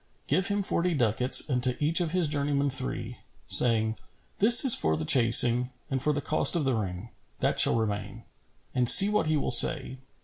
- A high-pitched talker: No, low, 130 Hz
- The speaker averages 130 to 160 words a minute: No, average, 195 wpm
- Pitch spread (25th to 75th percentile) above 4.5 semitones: Yes, wide, 5.6 semitones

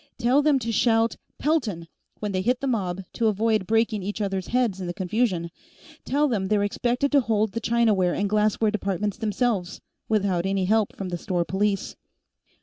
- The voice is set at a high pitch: Yes, high, 210 Hz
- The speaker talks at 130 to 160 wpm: No, average, 185 wpm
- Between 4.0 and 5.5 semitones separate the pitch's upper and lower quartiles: No, average, 3.4 semitones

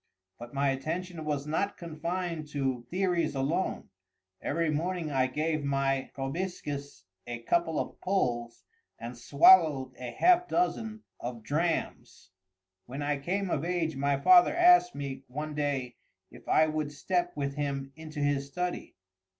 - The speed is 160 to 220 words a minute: No, average, 140 wpm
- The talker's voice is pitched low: No, medium, 150 Hz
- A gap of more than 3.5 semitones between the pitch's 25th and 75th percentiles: Yes, average, 4.3 semitones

